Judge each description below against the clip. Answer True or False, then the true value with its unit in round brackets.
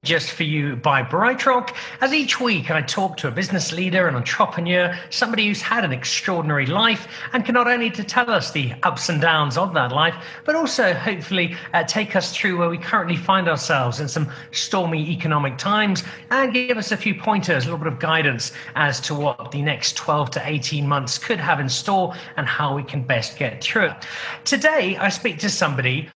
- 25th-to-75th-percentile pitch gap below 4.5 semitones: False (5.5 semitones)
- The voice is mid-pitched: True (170 Hz)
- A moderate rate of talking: False (210 wpm)